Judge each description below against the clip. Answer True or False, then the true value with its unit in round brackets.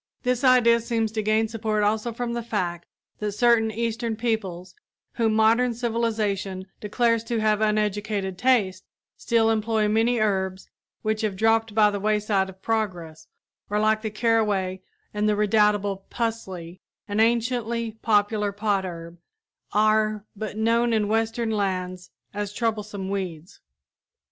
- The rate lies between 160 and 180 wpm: False (135 wpm)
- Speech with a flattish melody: True (2.0 semitones)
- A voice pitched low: False (215 Hz)